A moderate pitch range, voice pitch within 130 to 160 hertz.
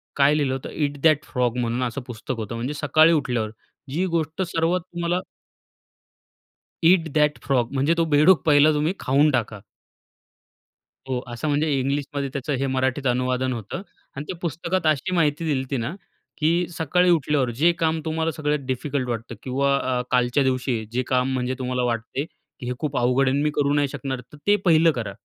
Yes: average, 3.6 semitones; medium, 140 Hz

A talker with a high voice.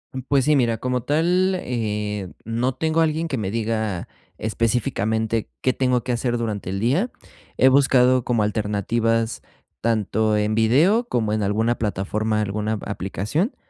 No: low, 115 Hz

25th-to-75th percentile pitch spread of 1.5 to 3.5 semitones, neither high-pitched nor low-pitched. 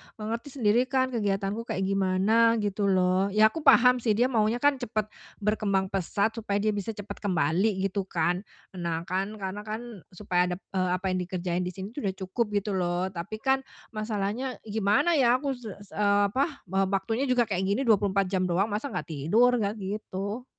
No: average, 3.2 semitones; high, 205 Hz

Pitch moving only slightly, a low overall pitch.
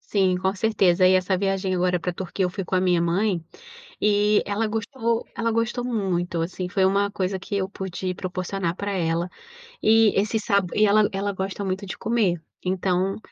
No: narrow, 2.2 semitones; high, 190 Hz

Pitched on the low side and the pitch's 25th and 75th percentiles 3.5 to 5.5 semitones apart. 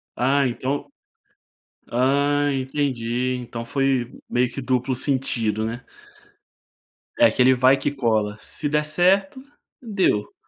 No: low, 130 Hz; average, 3.0 semitones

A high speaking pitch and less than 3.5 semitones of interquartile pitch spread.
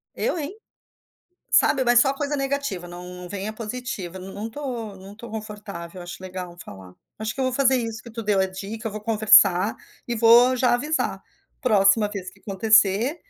No: high, 215 Hz; average, 4.2 semitones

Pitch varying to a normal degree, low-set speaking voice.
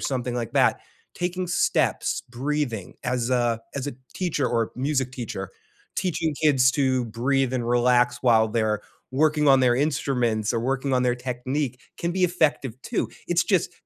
Yes: average, 3.5 semitones; low, 130 Hz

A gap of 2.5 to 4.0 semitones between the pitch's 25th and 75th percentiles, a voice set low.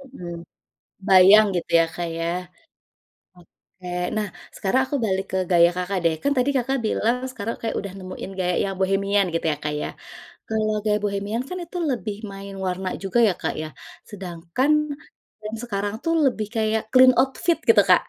No: average, 3.4 semitones; high, 200 Hz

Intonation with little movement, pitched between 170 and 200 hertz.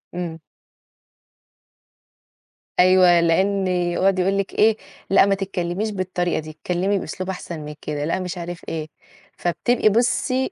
Yes: narrow, 2.2 semitones; medium, 185 Hz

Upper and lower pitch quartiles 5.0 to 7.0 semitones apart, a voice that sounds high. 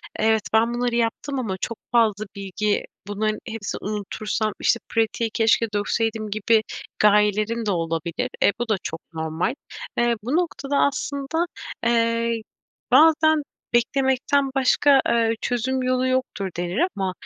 No: average, 3.5 semitones; high, 230 Hz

